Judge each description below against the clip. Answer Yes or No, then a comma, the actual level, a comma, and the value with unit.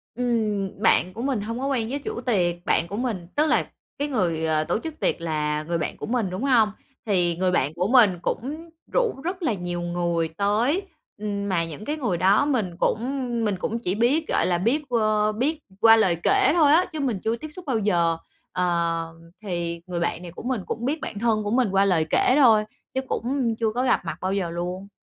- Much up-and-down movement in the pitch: Yes, wide, 6.2 semitones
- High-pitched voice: Yes, high, 210 Hz